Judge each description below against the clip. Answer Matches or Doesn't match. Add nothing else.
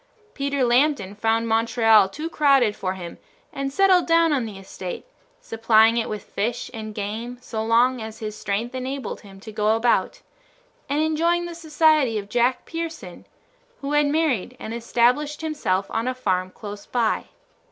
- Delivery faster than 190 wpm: Doesn't match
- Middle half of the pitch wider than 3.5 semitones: Matches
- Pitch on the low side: Doesn't match